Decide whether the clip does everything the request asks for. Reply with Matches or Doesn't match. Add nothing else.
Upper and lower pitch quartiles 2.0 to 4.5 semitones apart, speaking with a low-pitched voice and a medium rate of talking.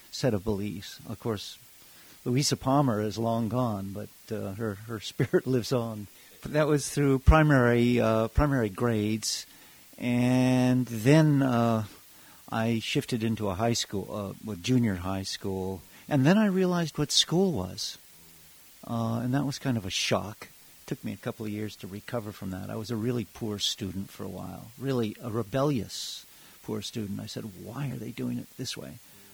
Matches